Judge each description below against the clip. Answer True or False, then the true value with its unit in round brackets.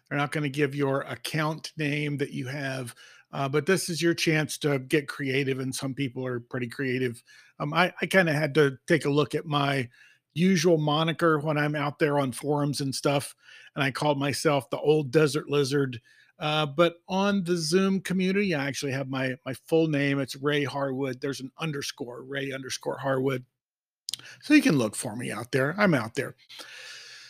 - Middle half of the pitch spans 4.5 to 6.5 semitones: False (2.6 semitones)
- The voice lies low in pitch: False (145 Hz)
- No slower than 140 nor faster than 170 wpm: False (195 wpm)